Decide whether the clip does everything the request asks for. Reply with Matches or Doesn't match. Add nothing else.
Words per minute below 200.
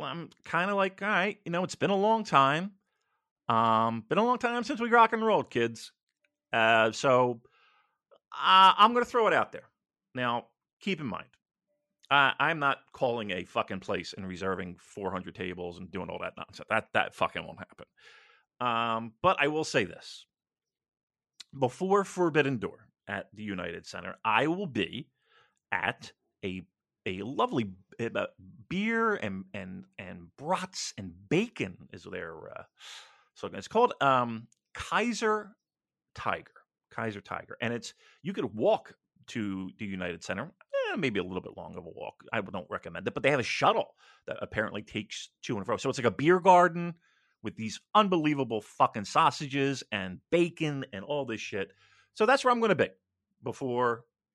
Matches